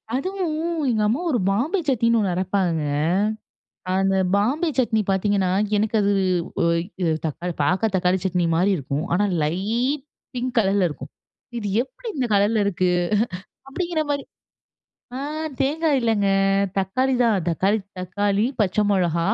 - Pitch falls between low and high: No, high, 205 Hz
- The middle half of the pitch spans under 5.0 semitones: No, wide, 5.5 semitones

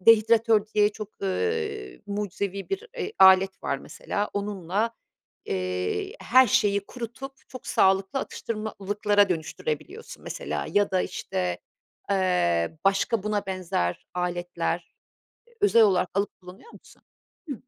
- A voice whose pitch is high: Yes, high, 200 Hz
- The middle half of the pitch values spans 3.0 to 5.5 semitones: Yes, average, 3.8 semitones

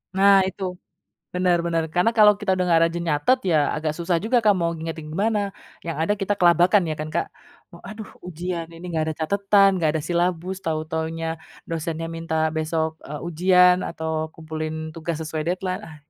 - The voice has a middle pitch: Yes, medium, 170 Hz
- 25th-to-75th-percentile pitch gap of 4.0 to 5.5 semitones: No, narrow, 2.5 semitones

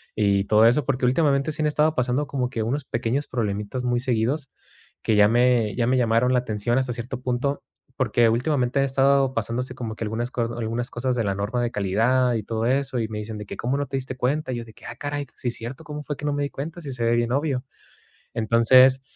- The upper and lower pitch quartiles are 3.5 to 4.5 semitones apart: No, average, 3.0 semitones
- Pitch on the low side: Yes, low, 125 Hz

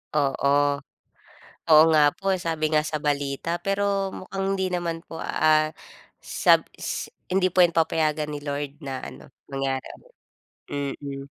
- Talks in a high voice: No, medium, 155 Hz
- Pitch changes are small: No, average, 3.8 semitones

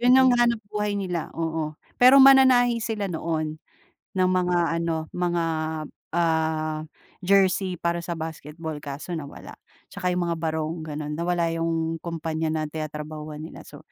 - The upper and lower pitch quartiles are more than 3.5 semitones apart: No, average, 2.8 semitones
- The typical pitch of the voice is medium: Yes, medium, 165 Hz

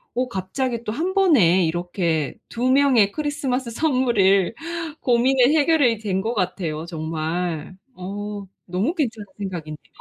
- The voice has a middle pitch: No, high, 210 Hz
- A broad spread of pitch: Yes, wide, 6.2 semitones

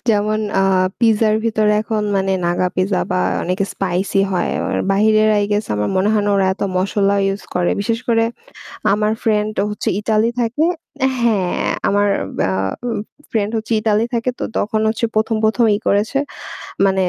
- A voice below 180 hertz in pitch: No, high, 210 Hz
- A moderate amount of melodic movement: No, narrow, 2.0 semitones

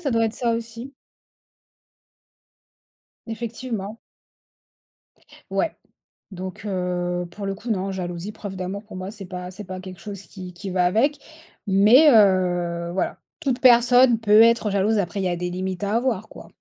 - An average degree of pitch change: Yes, average, 3.7 semitones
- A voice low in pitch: No, high, 200 Hz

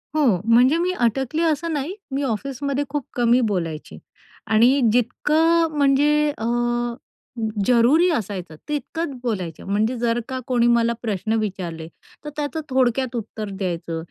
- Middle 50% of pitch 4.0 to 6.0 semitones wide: Yes, average, 5.2 semitones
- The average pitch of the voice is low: No, high, 245 Hz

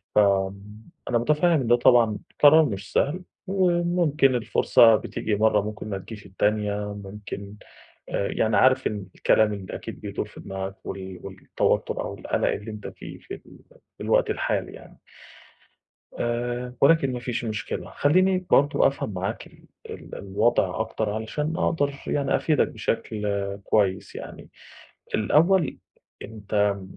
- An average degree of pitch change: No, wide, 5.7 semitones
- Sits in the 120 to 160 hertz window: No, low, 110 Hz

